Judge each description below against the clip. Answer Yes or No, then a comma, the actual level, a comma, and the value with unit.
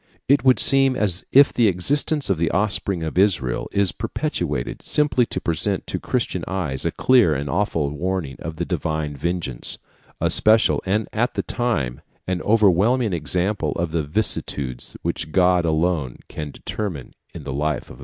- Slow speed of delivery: No, average, 175 wpm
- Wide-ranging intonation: Yes, wide, 5.8 semitones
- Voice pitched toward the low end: Yes, very low, 90 Hz